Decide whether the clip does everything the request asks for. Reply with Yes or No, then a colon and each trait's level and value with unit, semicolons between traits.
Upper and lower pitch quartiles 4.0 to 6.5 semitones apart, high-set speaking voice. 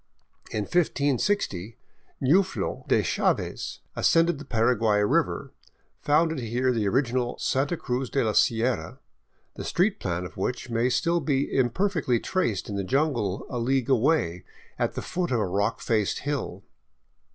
No: average, 5.1 semitones; low, 125 Hz